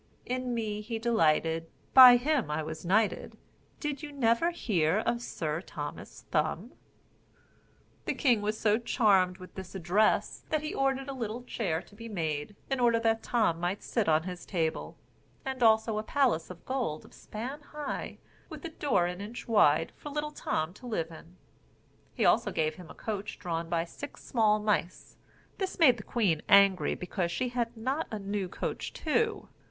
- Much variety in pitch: Yes, wide, 6.2 semitones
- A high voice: Yes, high, 215 Hz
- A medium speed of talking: Yes, average, 180 wpm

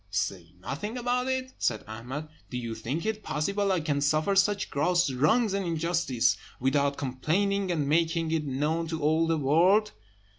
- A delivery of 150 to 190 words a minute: Yes, average, 170 wpm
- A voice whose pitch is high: No, medium, 160 Hz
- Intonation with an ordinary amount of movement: No, wide, 5.9 semitones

